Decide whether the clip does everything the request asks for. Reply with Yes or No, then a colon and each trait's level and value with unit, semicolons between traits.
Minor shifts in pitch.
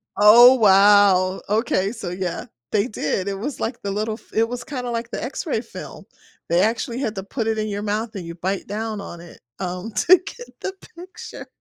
No: average, 3.4 semitones